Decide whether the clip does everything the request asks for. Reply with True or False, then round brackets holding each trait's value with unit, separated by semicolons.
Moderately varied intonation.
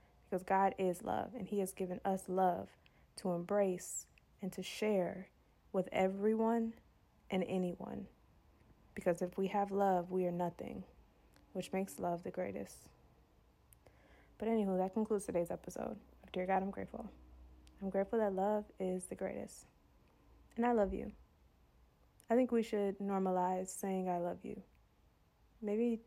False (2.2 semitones)